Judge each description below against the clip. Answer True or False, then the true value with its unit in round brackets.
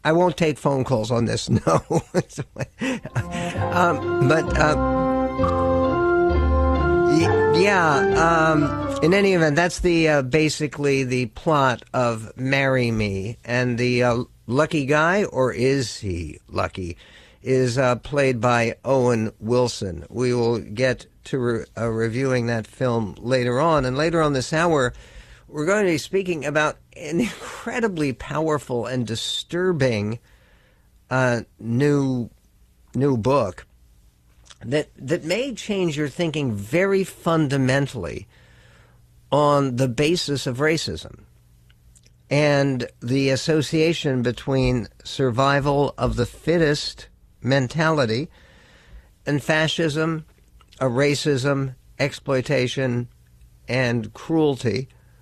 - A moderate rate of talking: False (110 wpm)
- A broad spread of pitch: False (4.6 semitones)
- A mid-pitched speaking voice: False (130 Hz)